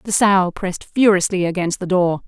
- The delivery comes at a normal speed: Yes, average, 185 wpm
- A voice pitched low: No, medium, 185 Hz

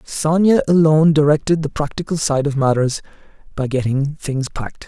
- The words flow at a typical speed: Yes, average, 150 wpm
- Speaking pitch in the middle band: Yes, medium, 150 Hz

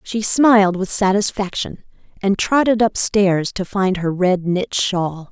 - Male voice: No, female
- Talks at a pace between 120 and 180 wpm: Yes, average, 145 wpm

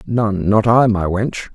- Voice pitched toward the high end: No, low, 105 Hz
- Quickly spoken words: No, average, 155 wpm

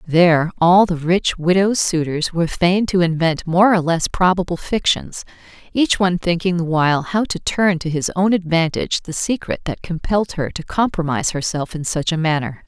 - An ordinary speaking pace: Yes, average, 185 wpm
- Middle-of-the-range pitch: Yes, medium, 175 Hz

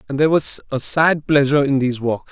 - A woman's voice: No, male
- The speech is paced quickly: Yes, fast, 235 wpm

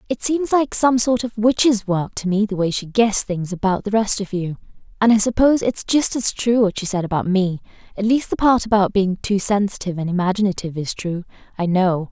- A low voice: No, high, 205 Hz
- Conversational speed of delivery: No, fast, 225 wpm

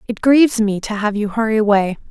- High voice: Yes, high, 215 Hz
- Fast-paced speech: Yes, fast, 230 wpm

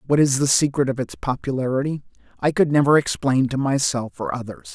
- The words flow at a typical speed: Yes, average, 190 wpm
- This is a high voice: No, low, 135 Hz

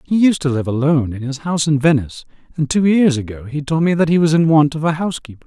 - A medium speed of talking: No, fast, 275 wpm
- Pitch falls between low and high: Yes, medium, 150 Hz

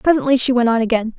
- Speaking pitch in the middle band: No, high, 245 Hz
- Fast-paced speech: Yes, fast, 255 wpm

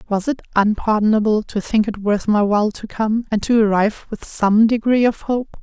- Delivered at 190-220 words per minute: Yes, fast, 205 wpm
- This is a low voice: No, high, 215 Hz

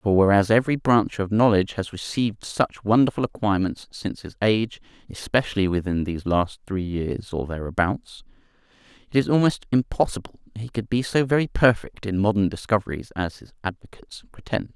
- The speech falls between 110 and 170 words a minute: Yes, average, 160 wpm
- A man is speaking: Yes, male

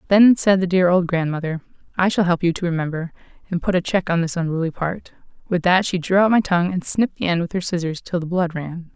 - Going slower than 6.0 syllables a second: No, 6.1 syllables/s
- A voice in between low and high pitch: Yes, medium, 175 Hz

